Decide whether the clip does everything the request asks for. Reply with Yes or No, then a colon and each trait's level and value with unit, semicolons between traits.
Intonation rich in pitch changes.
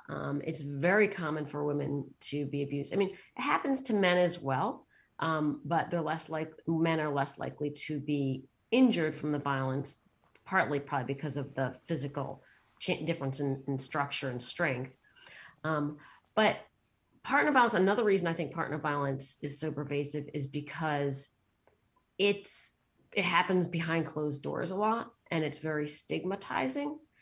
No: average, 2.8 semitones